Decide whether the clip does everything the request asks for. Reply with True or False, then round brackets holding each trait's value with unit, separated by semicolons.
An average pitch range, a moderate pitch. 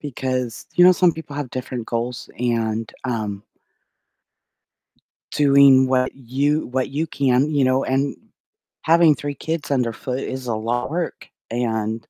False (3.2 semitones; 130 Hz)